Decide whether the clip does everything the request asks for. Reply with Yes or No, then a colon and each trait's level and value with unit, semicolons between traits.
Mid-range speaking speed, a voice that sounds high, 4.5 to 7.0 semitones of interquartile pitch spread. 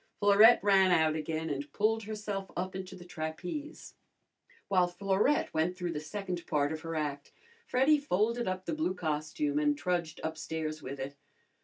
No: average, 165 wpm; medium, 180 Hz; average, 4.8 semitones